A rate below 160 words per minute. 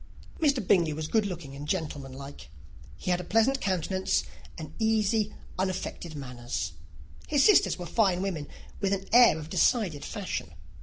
Yes: average, 150 wpm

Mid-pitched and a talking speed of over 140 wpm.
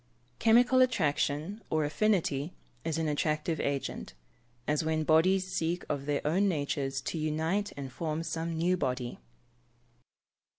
No: medium, 160 Hz; slow, 135 wpm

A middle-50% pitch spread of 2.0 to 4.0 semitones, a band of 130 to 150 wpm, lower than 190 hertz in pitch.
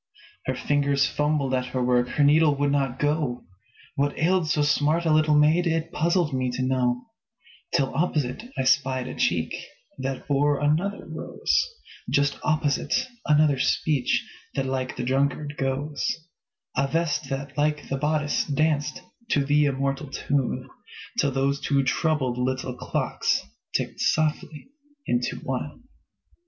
Yes: narrow, 2.4 semitones; average, 145 wpm; medium, 140 Hz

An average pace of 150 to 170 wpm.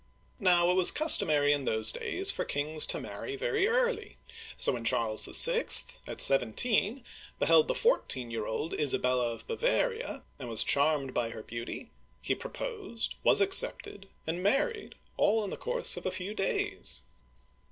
Yes: average, 165 wpm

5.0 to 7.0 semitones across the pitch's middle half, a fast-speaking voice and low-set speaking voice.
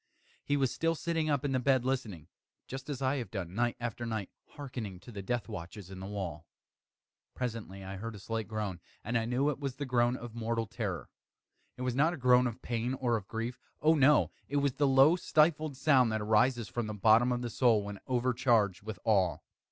No: average, 3.8 semitones; fast, 215 wpm; low, 120 Hz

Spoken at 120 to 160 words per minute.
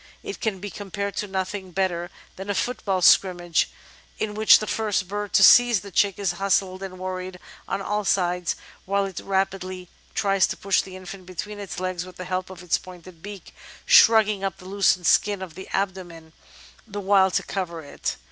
No: average, 190 wpm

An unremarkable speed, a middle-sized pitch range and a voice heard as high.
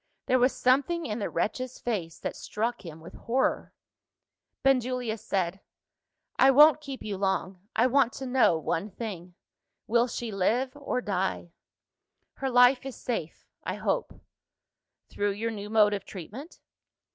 Yes: average, 145 wpm; average, 4.5 semitones; high, 230 Hz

